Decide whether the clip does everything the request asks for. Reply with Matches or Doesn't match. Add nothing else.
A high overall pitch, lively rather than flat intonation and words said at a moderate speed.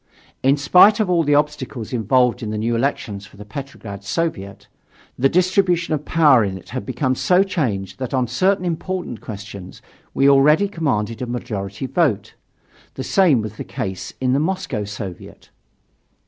Doesn't match